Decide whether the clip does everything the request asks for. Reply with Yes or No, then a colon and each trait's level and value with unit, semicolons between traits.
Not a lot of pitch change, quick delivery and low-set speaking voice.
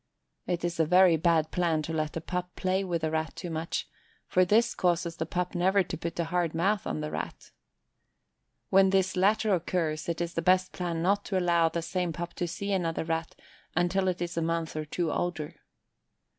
No: narrow, 2.1 semitones; fast, 210 wpm; medium, 175 Hz